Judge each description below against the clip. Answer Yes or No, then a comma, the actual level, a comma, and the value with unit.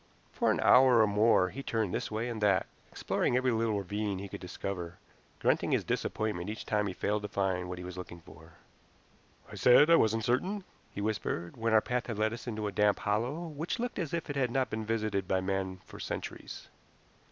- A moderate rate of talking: No, fast, 215 wpm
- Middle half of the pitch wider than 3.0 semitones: Yes, average, 3.9 semitones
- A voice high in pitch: No, low, 105 Hz